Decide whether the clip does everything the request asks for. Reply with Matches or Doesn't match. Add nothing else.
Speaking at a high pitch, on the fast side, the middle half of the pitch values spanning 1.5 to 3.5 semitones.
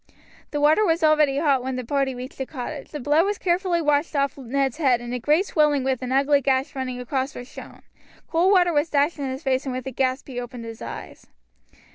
Matches